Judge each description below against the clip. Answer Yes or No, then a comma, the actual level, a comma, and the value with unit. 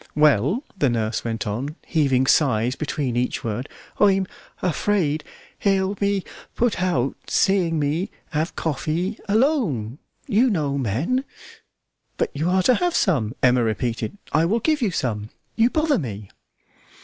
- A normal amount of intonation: No, wide, 8.1 semitones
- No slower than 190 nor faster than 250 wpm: No, average, 145 wpm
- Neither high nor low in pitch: Yes, medium, 155 Hz